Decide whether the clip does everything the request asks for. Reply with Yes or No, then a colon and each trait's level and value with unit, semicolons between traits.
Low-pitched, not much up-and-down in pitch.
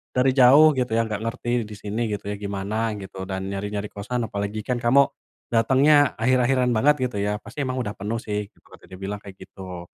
No: low, 110 Hz; average, 3.8 semitones